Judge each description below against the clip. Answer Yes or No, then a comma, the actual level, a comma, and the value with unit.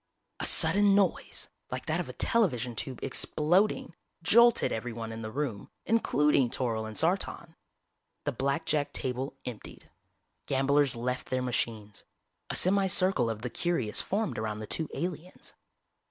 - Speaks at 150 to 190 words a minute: No, average, 140 wpm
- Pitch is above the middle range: No, low, 135 Hz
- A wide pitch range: Yes, wide, 7.1 semitones